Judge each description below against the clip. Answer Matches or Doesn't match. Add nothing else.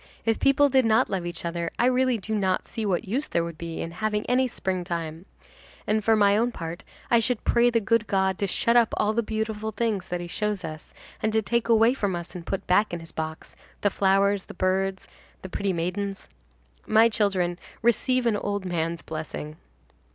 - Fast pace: Matches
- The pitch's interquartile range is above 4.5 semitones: Doesn't match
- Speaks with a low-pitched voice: Doesn't match